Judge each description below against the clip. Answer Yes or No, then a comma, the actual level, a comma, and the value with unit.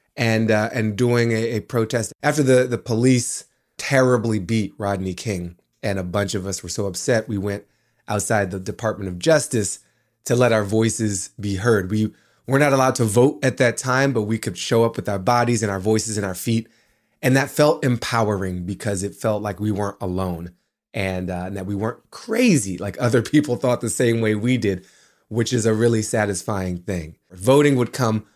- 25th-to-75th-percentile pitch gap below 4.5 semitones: Yes, average, 3.3 semitones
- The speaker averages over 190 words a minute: Yes, average, 200 wpm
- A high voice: No, low, 110 Hz